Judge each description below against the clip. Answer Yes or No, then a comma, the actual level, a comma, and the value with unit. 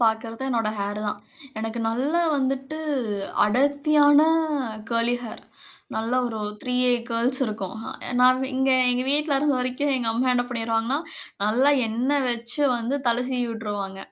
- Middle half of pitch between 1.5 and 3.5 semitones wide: Yes, average, 2.9 semitones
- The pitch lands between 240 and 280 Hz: Yes, high, 245 Hz